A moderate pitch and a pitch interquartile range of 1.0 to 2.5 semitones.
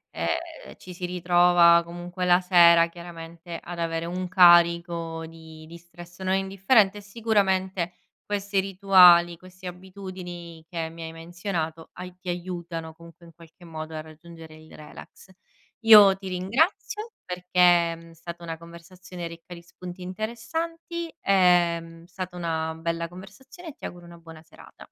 Yes: medium, 175 Hz; narrow, 2.1 semitones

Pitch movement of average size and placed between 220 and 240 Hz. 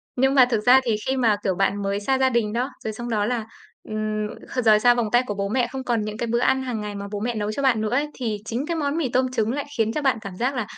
Yes: average, 3.3 semitones; high, 235 Hz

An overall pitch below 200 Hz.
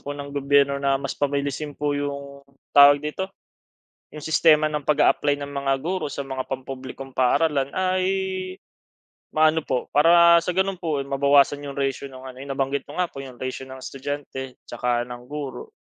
Yes: medium, 140 Hz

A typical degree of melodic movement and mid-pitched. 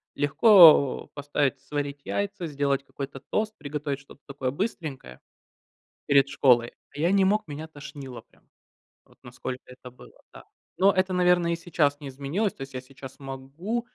Yes: average, 4.5 semitones; medium, 145 Hz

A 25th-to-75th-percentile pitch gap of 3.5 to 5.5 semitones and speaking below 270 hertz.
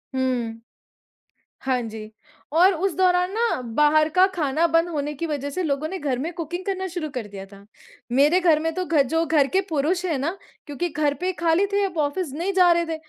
No: average, 4.2 semitones; very high, 320 Hz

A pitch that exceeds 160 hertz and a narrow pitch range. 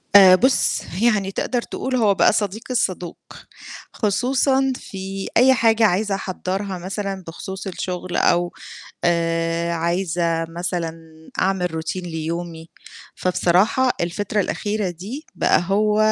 No: high, 190 Hz; average, 3.6 semitones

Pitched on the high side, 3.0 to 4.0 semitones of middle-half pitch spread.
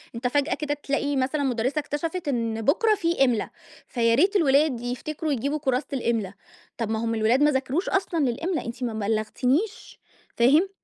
No: very high, 275 Hz; average, 4.6 semitones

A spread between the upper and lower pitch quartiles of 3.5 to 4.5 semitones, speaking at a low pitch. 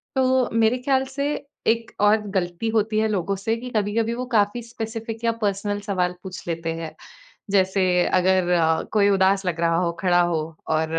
No: average, 4.2 semitones; high, 205 Hz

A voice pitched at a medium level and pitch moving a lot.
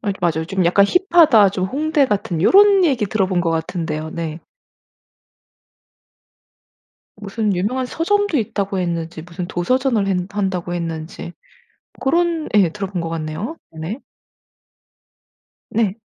No: high, 195 Hz; wide, 7.0 semitones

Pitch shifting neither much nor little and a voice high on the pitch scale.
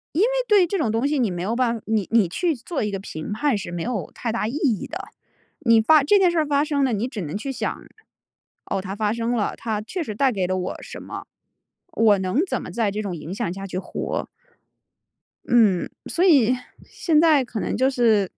No: wide, 5.8 semitones; high, 230 Hz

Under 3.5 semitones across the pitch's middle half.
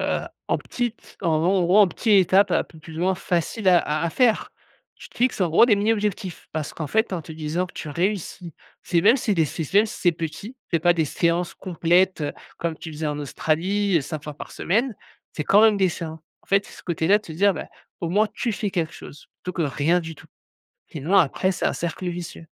No: average, 3.9 semitones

